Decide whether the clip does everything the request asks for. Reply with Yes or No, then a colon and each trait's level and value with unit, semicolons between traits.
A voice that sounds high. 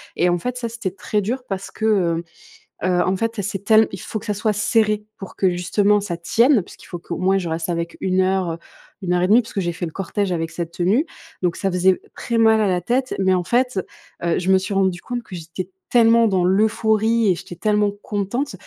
Yes: high, 195 Hz